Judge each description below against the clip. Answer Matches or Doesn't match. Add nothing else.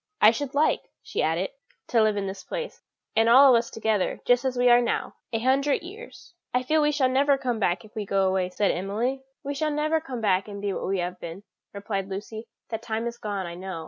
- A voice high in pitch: Matches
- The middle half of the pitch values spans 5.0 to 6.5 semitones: Matches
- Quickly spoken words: Matches